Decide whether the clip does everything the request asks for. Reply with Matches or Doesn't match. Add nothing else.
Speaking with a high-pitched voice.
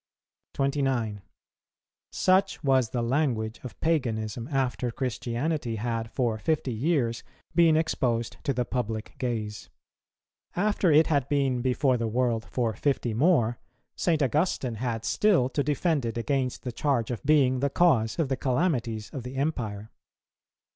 Doesn't match